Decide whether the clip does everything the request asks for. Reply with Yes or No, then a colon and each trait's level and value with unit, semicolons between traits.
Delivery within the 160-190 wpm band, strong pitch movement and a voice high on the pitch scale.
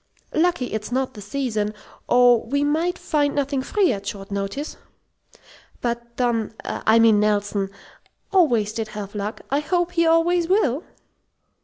No: average, 145 wpm; wide, 6.2 semitones; high, 245 Hz